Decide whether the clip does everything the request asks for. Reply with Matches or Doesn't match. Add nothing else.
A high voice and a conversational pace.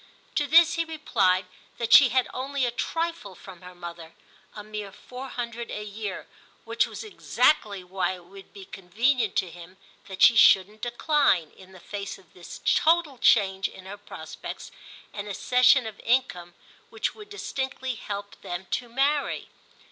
Matches